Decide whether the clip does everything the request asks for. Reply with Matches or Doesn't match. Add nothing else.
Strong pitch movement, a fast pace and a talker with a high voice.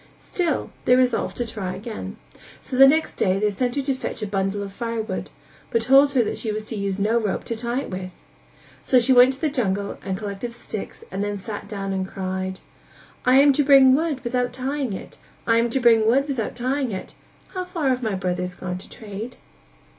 Doesn't match